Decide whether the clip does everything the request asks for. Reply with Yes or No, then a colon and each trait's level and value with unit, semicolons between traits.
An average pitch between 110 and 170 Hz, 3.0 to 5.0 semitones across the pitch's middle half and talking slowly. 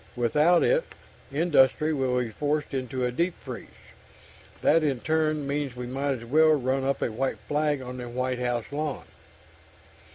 No: low, 135 Hz; average, 3.4 semitones; average, 165 wpm